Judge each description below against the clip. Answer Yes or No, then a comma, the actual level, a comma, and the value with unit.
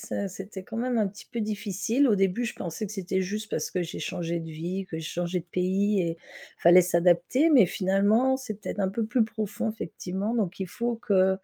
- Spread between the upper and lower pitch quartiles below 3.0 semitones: No, average, 3.4 semitones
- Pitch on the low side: No, high, 195 Hz